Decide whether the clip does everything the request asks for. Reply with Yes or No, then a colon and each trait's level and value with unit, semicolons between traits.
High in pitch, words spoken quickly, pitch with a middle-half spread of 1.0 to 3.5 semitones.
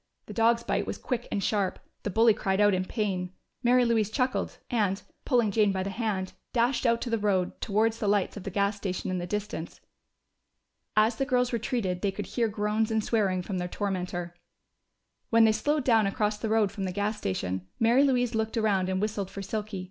Yes: high, 210 Hz; fast, 210 wpm; average, 3.0 semitones